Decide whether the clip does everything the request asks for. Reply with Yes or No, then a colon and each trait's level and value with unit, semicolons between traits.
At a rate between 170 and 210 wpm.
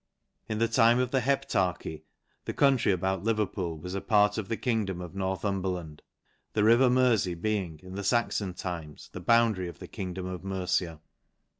Yes: average, 180 wpm